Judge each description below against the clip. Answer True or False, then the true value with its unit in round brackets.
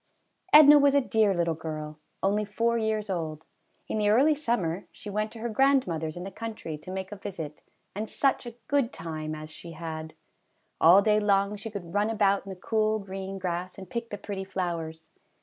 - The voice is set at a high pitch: True (195 Hz)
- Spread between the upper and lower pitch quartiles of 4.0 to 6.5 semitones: True (4.5 semitones)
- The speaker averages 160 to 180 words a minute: False (200 wpm)